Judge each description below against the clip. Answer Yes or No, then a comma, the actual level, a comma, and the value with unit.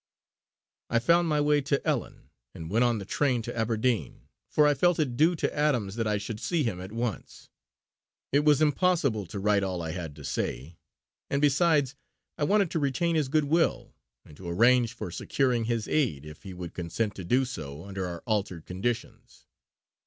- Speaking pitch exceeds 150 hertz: No, low, 120 Hz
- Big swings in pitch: Yes, wide, 7.4 semitones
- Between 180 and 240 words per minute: Yes, average, 190 wpm